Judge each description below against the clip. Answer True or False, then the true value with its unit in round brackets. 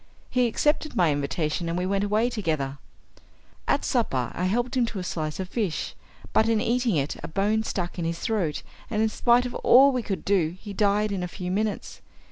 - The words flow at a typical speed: False (210 wpm)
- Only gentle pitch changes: False (4.6 semitones)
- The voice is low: False (200 Hz)